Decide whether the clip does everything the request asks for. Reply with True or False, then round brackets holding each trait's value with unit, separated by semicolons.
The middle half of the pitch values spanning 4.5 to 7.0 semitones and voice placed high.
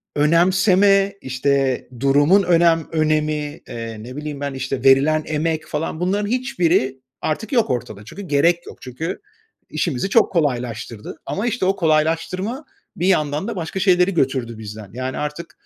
False (5.4 semitones; 155 Hz)